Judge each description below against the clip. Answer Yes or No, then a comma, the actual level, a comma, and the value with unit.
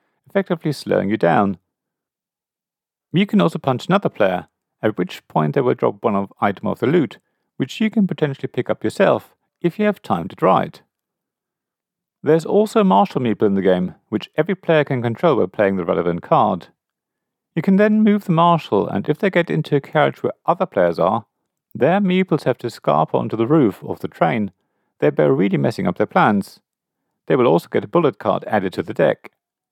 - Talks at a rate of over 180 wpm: Yes, average, 200 wpm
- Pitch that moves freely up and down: Yes, wide, 8.8 semitones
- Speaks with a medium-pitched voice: Yes, medium, 155 Hz